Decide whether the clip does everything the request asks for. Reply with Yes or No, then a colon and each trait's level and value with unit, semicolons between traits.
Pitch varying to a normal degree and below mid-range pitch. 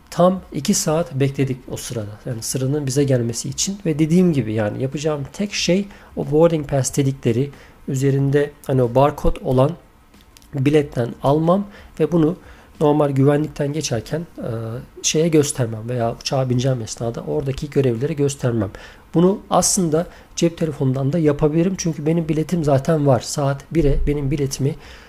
No: average, 3.2 semitones; medium, 145 Hz